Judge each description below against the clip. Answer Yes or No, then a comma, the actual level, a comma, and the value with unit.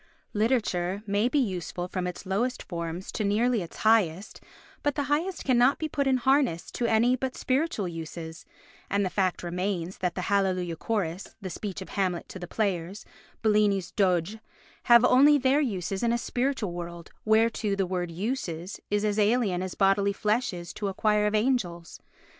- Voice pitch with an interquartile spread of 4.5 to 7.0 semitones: Yes, average, 4.8 semitones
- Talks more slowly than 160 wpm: No, average, 175 wpm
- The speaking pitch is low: No, high, 200 Hz